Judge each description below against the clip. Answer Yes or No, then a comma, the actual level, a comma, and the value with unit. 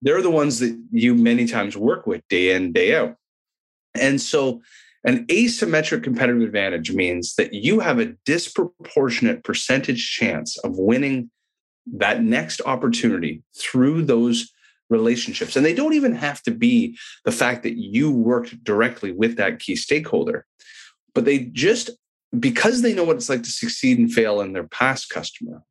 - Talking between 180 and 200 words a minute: No, average, 160 wpm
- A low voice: No, medium, 145 Hz